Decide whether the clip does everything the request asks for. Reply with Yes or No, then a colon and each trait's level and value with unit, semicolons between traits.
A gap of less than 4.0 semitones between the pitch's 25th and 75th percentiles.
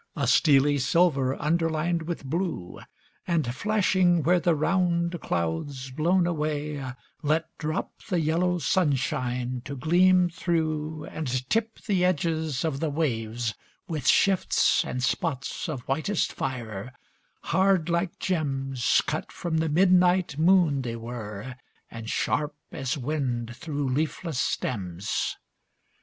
No: average, 4.9 semitones